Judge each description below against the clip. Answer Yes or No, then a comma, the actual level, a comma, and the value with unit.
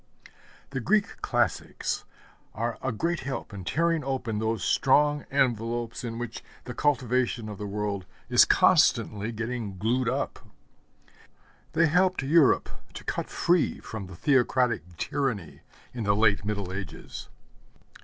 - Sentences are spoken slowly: Yes, slow, 130 wpm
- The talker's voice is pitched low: Yes, low, 120 Hz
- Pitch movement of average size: Yes, average, 4.5 semitones